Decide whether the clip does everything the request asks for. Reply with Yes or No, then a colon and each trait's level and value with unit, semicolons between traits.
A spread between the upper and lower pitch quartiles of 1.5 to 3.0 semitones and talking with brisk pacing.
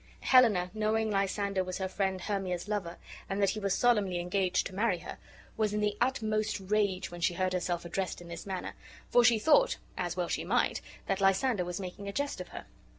Yes: average, 2.7 semitones; fast, 210 wpm